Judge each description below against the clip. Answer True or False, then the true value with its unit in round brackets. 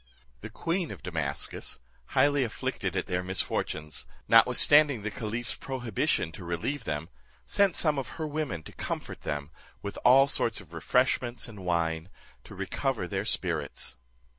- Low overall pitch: True (110 Hz)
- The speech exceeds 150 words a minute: False (145 wpm)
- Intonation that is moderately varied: False (8.2 semitones)